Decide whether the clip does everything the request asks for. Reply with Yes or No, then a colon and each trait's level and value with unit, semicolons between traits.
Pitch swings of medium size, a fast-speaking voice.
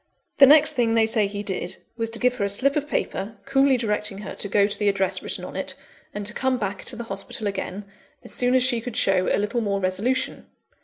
Yes: average, 3.9 semitones; fast, 245 wpm